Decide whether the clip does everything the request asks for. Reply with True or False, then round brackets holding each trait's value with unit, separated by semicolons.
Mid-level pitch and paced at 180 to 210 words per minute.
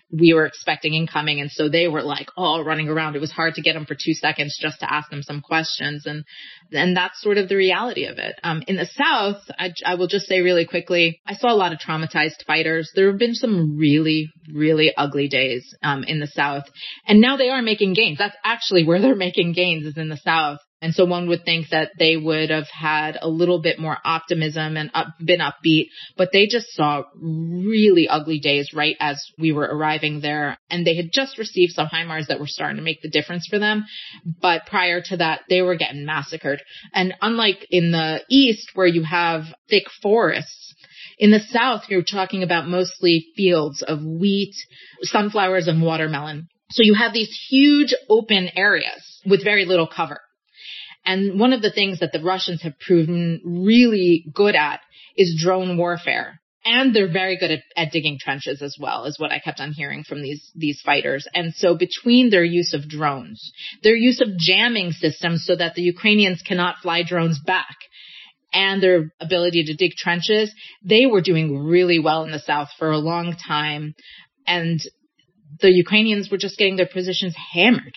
True (170 Hz; 195 wpm)